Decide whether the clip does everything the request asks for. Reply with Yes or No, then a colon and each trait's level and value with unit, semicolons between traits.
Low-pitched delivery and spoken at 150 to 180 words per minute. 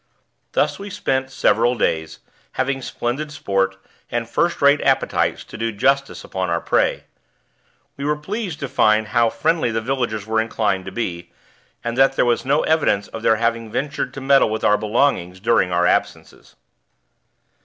Yes: low, 115 Hz; average, 165 wpm